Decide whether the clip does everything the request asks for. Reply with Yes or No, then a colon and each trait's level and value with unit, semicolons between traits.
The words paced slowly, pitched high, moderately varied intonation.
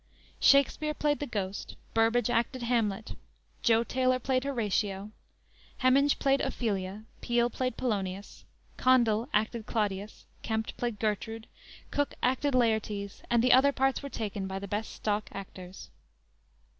Yes: slow, 130 wpm; high, 225 Hz; average, 3.7 semitones